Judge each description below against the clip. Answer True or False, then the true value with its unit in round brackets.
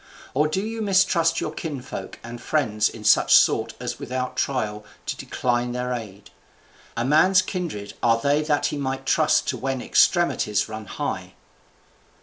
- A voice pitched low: True (130 Hz)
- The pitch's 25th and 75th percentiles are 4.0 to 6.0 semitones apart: True (5.2 semitones)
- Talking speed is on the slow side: False (155 wpm)